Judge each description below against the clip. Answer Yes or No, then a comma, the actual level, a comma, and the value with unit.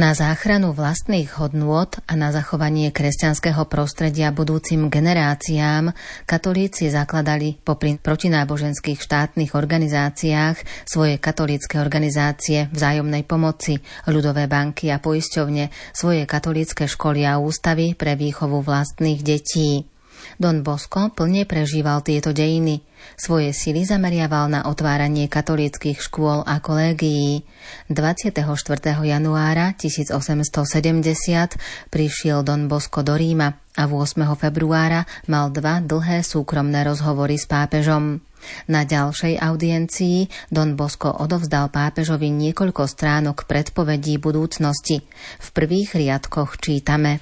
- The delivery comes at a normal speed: No, slow, 105 wpm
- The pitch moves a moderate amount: No, narrow, 1.5 semitones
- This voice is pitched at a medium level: Yes, medium, 150 Hz